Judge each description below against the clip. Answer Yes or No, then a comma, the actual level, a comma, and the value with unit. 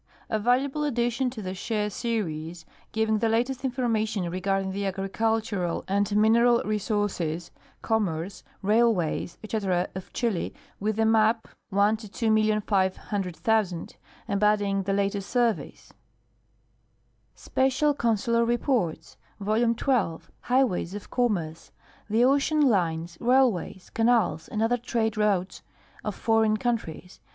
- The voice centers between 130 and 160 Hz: No, high, 215 Hz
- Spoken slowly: Yes, slow, 110 wpm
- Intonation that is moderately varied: Yes, average, 3.5 semitones